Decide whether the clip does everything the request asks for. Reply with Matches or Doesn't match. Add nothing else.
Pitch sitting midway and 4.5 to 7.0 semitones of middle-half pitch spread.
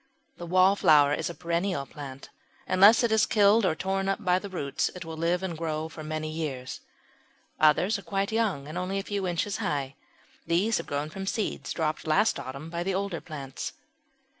Doesn't match